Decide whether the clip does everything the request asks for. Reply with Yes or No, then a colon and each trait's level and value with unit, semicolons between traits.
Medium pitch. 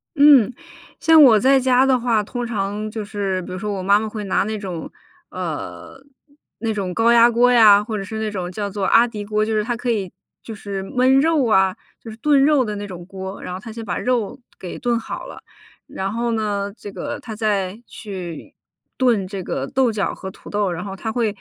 No: high, 215 Hz